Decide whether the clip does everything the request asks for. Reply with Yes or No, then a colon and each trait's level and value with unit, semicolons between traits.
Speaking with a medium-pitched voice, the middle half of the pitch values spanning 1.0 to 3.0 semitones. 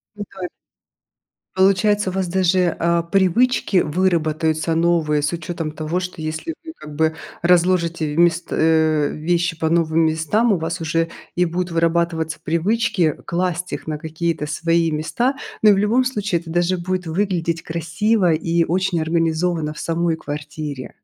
Yes: medium, 170 Hz; narrow, 2.4 semitones